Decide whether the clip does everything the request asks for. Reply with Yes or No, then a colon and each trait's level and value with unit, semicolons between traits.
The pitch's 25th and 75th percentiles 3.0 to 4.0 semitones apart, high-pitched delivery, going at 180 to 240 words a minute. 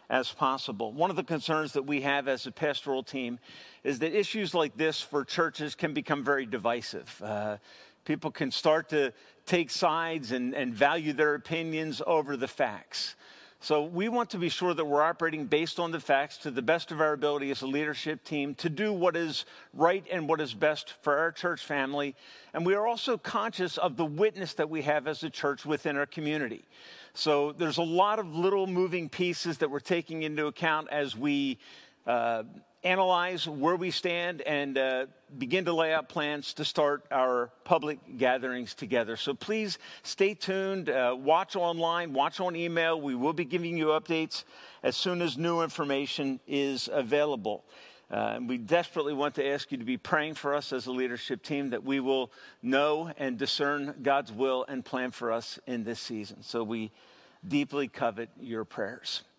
No: average, 3.6 semitones; medium, 150 Hz; average, 190 wpm